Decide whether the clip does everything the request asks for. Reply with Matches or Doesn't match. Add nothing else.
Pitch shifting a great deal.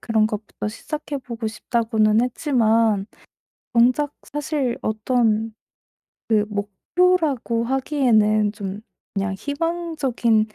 Doesn't match